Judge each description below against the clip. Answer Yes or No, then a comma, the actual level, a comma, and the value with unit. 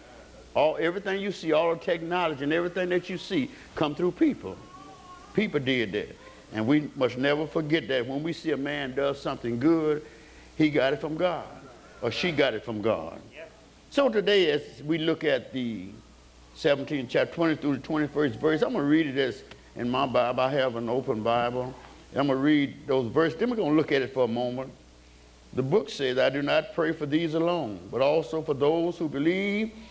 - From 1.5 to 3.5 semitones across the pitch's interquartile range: No, average, 4.0 semitones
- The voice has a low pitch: No, medium, 150 Hz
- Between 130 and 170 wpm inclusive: No, average, 200 wpm